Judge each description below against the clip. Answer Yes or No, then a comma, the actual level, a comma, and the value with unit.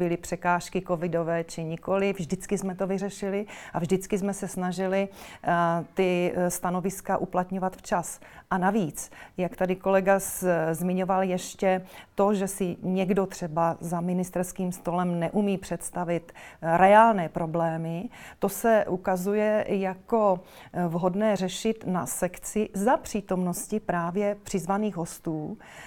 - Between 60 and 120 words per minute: Yes, slow, 115 wpm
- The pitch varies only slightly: Yes, narrow, 2.1 semitones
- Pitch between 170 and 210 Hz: Yes, medium, 185 Hz